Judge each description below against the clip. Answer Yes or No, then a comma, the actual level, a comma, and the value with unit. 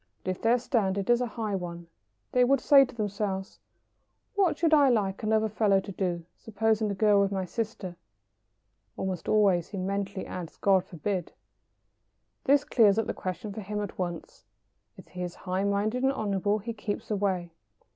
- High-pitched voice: Yes, high, 205 Hz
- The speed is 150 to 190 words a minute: Yes, average, 175 wpm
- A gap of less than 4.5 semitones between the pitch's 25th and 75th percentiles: Yes, average, 2.8 semitones